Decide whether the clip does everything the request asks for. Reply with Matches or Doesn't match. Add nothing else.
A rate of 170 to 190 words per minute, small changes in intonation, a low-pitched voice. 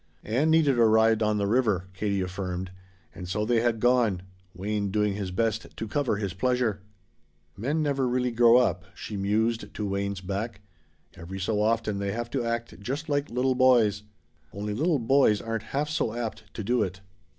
Doesn't match